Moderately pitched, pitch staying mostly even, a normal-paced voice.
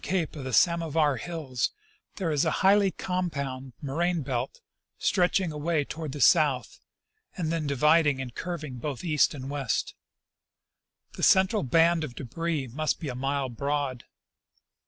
No: medium, 150 Hz; average, 3.9 semitones; average, 150 wpm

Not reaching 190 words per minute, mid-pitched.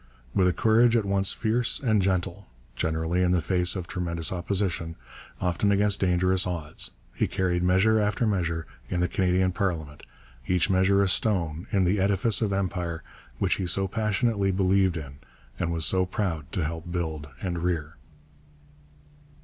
No: average, 160 wpm; very low, 90 Hz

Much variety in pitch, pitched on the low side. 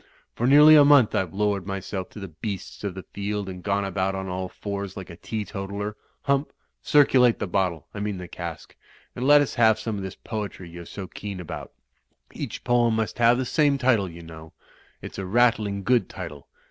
No: average, 3.9 semitones; low, 100 Hz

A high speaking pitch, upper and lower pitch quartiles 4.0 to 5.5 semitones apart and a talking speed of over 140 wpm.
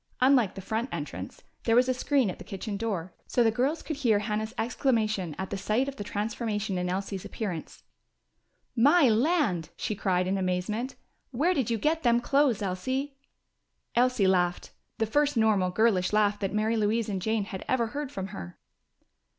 Yes: high, 220 Hz; average, 4.5 semitones; average, 180 wpm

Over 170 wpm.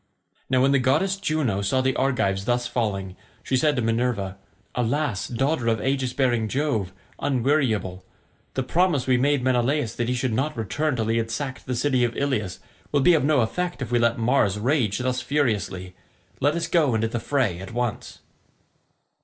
Yes: average, 185 wpm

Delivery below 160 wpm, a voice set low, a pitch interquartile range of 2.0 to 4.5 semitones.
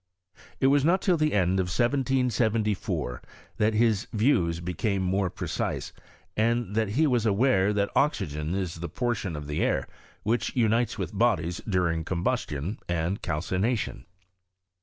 No: average, 145 wpm; low, 105 Hz; wide, 5.4 semitones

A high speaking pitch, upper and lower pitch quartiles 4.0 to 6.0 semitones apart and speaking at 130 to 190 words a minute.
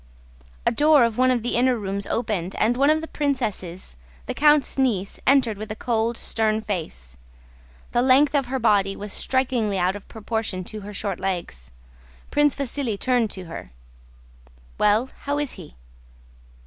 Yes: high, 225 Hz; average, 4.7 semitones; average, 165 wpm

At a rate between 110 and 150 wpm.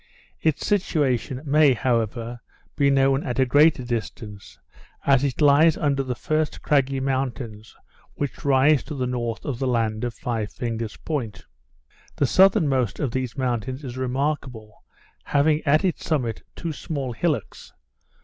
Yes: average, 145 wpm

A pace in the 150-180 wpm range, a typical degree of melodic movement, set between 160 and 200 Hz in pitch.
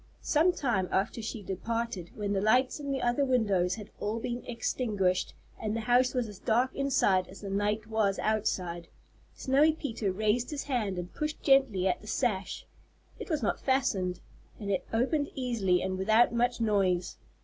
No: average, 175 wpm; average, 4.5 semitones; high, 220 Hz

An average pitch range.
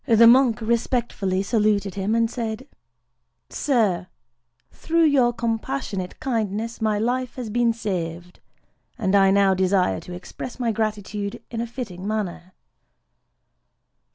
Yes: average, 3.8 semitones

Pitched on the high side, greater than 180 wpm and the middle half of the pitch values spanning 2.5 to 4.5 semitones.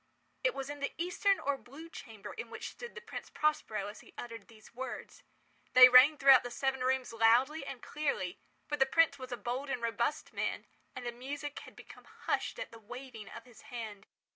Yes: very high, 255 Hz; fast, 205 wpm; average, 3.8 semitones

